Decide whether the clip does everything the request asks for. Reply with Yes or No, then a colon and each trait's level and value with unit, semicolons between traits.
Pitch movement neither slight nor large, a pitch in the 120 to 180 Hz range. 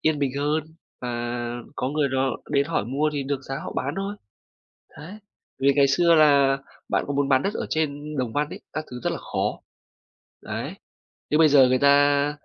No: narrow, 2.0 semitones; medium, 140 Hz